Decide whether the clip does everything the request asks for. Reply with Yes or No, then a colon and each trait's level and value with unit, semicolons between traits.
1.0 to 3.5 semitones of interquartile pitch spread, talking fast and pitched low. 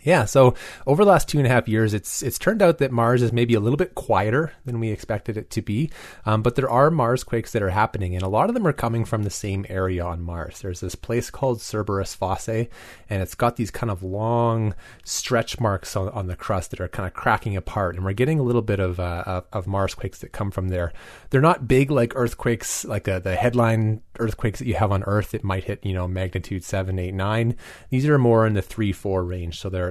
No: average, 4.0 semitones; fast, 250 wpm; low, 110 Hz